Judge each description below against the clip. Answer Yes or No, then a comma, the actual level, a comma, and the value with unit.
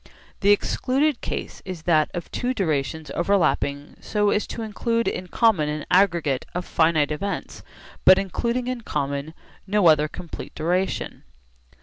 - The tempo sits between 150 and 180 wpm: No, average, 140 wpm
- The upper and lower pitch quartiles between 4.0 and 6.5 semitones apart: Yes, average, 5.2 semitones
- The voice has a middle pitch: Yes, medium, 180 Hz